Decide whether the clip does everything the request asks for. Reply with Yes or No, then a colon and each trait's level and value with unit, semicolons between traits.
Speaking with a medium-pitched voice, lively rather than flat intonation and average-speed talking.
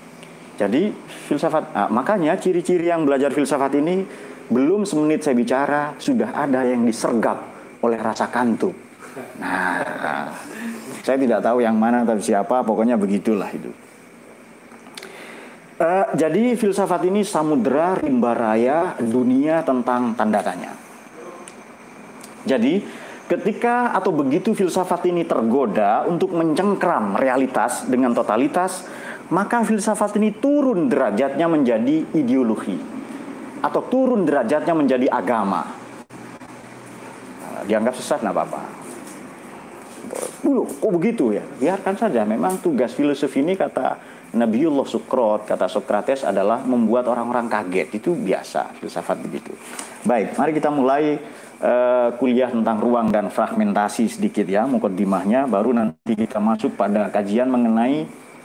Yes: medium, 145 Hz; wide, 8.6 semitones; average, 115 wpm